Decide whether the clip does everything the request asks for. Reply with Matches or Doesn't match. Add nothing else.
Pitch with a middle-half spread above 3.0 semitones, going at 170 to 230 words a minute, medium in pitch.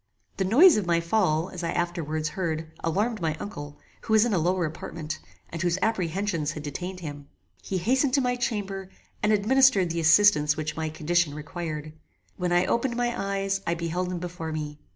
Matches